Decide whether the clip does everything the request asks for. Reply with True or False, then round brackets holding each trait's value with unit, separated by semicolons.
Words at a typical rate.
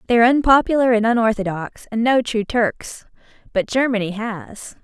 True (150 wpm)